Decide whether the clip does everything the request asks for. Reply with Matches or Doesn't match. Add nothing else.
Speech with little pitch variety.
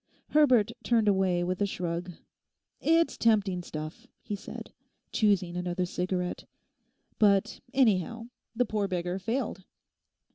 Doesn't match